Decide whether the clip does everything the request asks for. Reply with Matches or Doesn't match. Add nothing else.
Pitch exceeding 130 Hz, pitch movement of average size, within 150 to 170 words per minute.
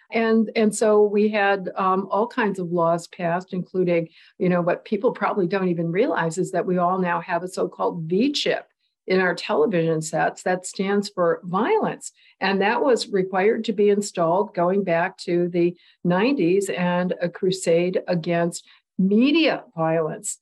Matches